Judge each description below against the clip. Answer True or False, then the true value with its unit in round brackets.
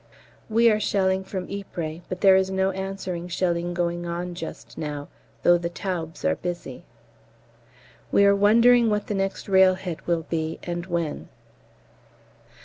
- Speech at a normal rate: True (145 wpm)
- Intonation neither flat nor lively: False (2.2 semitones)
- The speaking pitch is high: False (180 Hz)